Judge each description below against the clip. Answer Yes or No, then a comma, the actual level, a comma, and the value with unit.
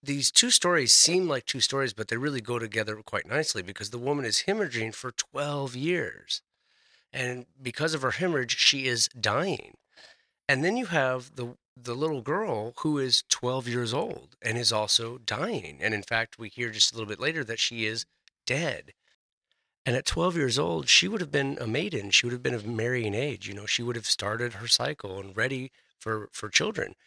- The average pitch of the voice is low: Yes, low, 120 Hz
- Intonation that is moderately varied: Yes, average, 3.7 semitones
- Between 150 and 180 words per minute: No, fast, 205 wpm